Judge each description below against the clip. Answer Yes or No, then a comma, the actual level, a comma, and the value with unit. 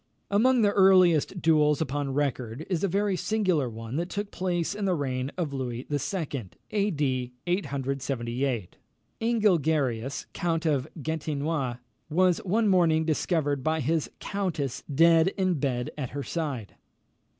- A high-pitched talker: No, medium, 155 Hz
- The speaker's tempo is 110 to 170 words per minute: Yes, average, 140 wpm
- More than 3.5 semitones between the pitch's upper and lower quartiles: Yes, average, 5.2 semitones